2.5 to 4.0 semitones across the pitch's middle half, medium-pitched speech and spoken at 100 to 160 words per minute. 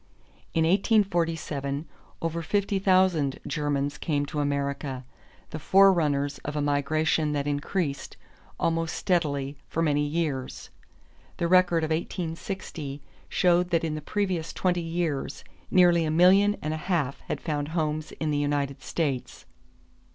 Yes: average, 3.2 semitones; medium, 155 Hz; slow, 135 wpm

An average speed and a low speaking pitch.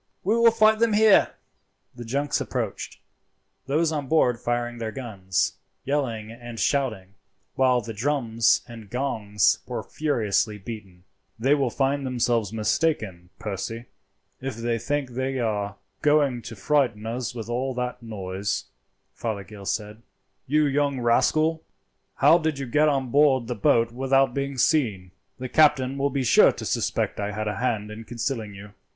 Yes: average, 155 wpm; low, 120 Hz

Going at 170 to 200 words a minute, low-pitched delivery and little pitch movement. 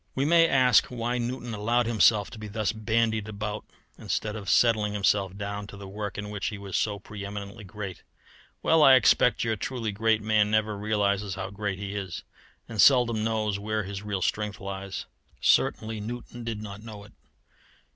Yes: average, 185 wpm; low, 105 Hz; narrow, 2.0 semitones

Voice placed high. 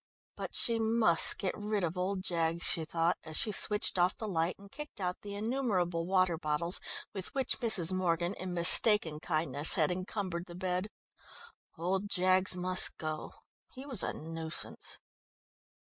No: medium, 180 Hz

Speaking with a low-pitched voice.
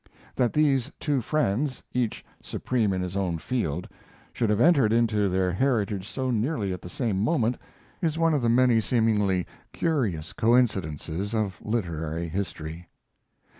Yes: low, 110 Hz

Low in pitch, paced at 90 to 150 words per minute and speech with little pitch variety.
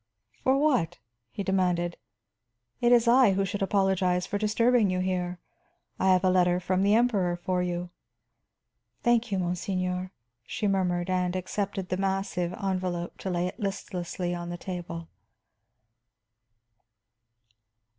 No: medium, 185 Hz; slow, 135 wpm; narrow, 1.9 semitones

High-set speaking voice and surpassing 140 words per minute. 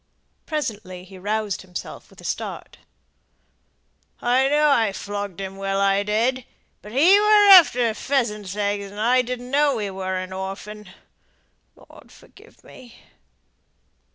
No: high, 210 Hz; slow, 135 wpm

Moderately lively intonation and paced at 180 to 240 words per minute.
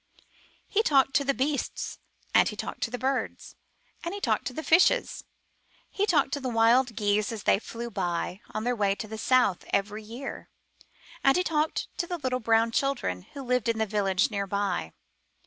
Yes: average, 4.8 semitones; average, 195 wpm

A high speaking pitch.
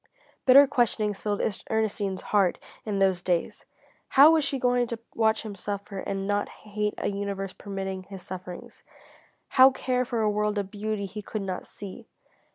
Yes: high, 205 Hz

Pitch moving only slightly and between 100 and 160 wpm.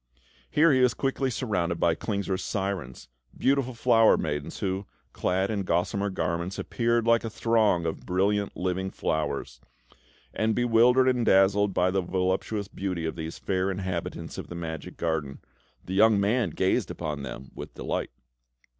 No: average, 4.6 semitones; average, 155 wpm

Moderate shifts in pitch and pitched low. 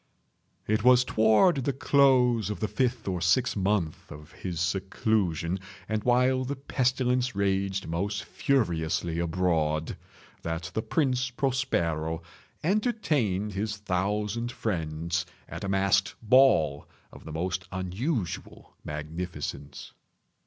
No: wide, 6.5 semitones; low, 100 Hz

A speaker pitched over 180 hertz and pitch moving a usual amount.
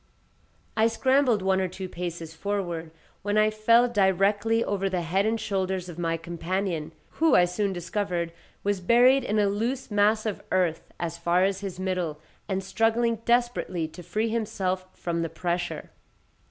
Yes: high, 190 Hz; average, 3.6 semitones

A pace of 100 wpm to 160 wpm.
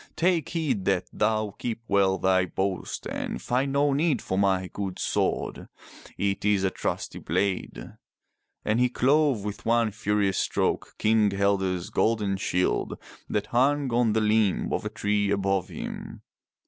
Yes: average, 150 wpm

